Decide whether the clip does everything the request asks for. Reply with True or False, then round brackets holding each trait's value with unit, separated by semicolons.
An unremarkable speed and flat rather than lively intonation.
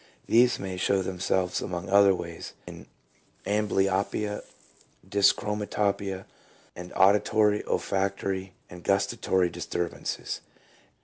False (90 wpm; 1.7 semitones)